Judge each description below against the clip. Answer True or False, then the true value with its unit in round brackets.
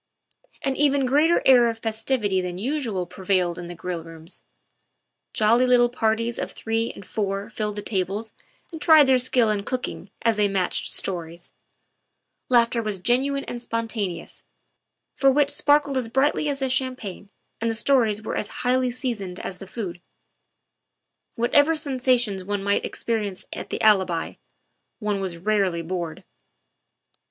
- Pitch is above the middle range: True (225 Hz)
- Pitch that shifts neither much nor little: True (4.8 semitones)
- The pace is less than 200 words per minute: True (150 wpm)